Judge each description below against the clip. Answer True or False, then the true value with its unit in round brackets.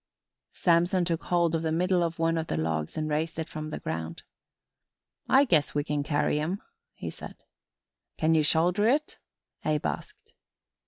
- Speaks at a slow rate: False (170 wpm)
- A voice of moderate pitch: True (160 Hz)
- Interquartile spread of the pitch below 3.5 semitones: True (2.5 semitones)